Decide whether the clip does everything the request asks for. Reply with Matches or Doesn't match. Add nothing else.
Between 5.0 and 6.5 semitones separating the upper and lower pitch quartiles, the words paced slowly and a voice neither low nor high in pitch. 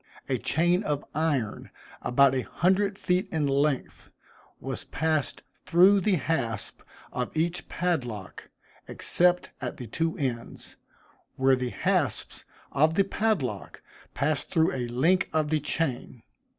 Matches